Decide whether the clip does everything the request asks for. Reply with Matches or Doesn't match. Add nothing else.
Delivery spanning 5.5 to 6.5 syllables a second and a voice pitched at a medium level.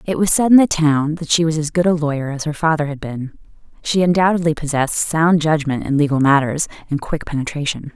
Matches